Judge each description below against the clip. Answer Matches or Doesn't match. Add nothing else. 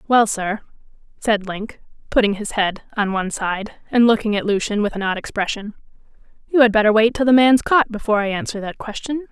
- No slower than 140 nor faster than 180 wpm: Doesn't match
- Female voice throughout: Matches